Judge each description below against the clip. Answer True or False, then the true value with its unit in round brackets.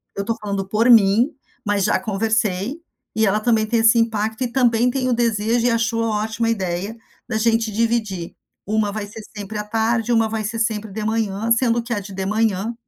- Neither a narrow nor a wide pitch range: False (1.8 semitones)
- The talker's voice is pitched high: True (220 Hz)